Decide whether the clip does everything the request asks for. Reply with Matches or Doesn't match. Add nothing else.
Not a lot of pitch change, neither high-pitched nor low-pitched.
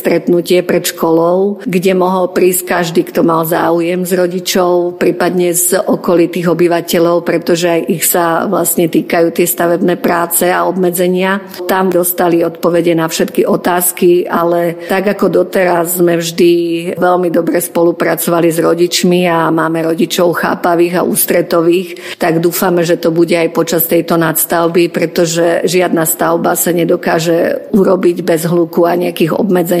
Matches